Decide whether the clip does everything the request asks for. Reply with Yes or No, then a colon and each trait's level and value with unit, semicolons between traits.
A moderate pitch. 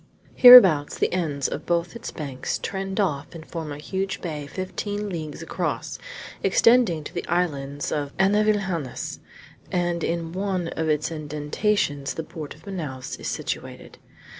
Yes: medium, 170 Hz